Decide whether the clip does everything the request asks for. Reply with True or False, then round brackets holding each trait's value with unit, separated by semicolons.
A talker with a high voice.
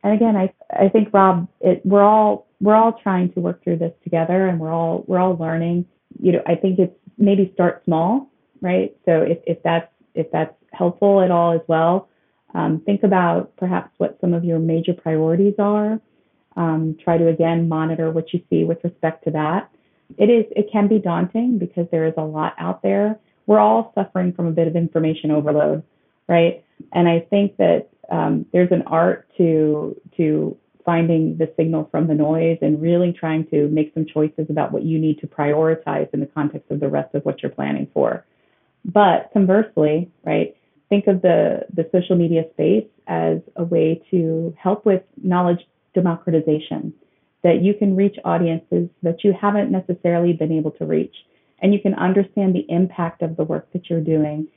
False (170 Hz)